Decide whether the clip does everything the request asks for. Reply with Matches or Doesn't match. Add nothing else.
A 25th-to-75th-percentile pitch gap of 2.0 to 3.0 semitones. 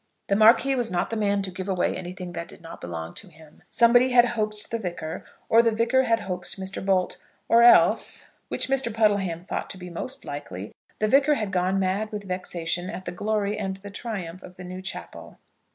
Doesn't match